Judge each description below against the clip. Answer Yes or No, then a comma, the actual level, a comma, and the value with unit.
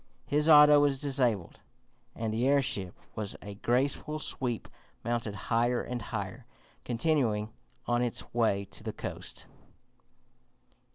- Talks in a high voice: No, low, 120 Hz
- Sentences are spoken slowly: Yes, slow, 120 wpm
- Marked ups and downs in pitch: No, average, 4.3 semitones